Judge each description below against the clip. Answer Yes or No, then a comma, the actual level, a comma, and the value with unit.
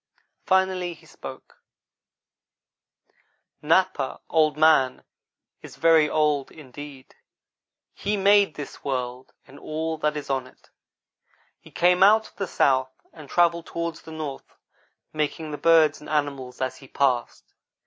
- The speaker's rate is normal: No, slow, 130 wpm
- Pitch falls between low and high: Yes, medium, 155 Hz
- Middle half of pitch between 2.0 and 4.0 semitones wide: Yes, average, 3.4 semitones